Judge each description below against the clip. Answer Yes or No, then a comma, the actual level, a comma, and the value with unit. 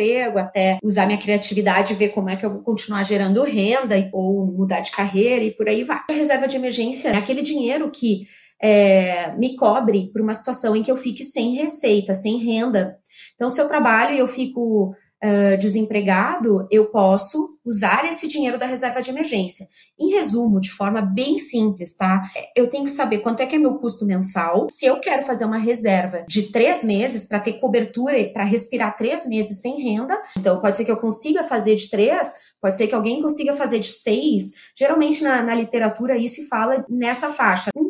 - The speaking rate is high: Yes, fast, 200 wpm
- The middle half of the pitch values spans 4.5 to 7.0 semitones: No, average, 4.1 semitones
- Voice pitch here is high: Yes, high, 225 Hz